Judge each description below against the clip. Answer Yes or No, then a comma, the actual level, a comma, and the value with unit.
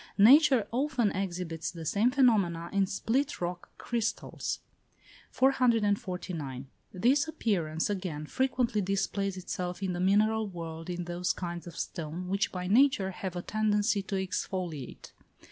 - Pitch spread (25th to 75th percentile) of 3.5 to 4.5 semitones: Yes, average, 4.1 semitones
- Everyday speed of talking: No, slow, 130 wpm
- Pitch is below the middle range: No, high, 195 Hz